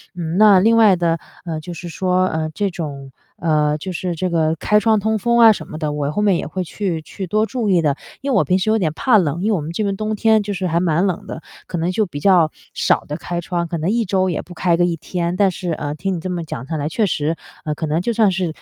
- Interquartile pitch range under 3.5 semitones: No, average, 3.9 semitones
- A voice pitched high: No, medium, 180 Hz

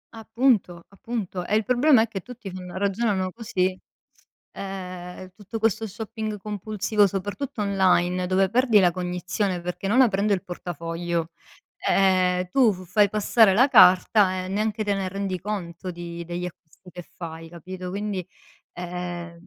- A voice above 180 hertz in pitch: Yes, high, 190 Hz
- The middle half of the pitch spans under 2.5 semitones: No, average, 2.9 semitones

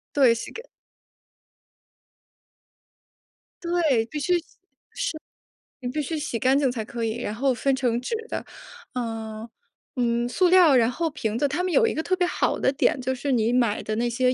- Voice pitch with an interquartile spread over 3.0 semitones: Yes, average, 4.5 semitones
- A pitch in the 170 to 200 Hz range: No, very high, 255 Hz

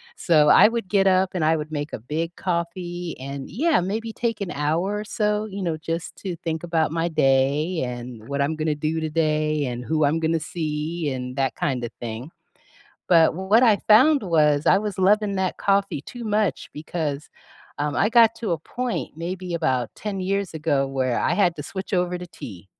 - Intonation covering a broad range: No, average, 4.6 semitones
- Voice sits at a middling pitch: Yes, medium, 165 Hz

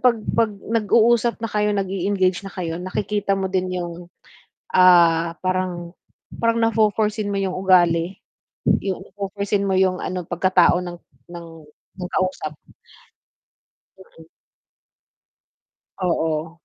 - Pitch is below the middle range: No, medium, 185 Hz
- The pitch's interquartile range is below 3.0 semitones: Yes, narrow, 2.6 semitones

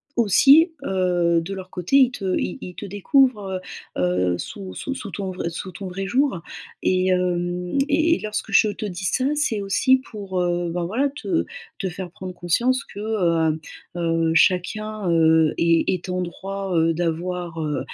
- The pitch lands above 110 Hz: Yes, medium, 185 Hz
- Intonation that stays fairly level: No, average, 3.6 semitones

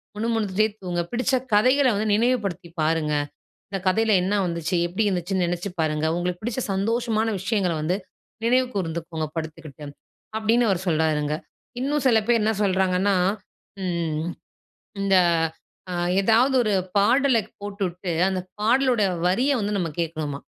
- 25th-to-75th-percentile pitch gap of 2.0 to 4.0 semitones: No, average, 4.7 semitones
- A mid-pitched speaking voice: No, high, 195 Hz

